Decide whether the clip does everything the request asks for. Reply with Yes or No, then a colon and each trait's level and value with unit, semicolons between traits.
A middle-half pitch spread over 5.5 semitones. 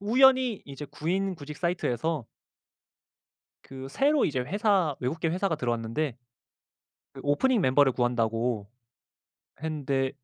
Yes: wide, 6.6 semitones